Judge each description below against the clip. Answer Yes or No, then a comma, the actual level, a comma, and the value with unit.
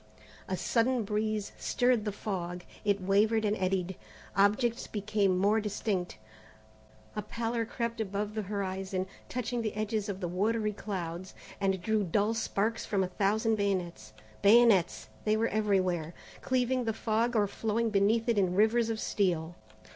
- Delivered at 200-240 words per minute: No, average, 150 wpm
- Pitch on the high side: Yes, high, 210 Hz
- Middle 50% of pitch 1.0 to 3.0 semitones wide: Yes, average, 2.7 semitones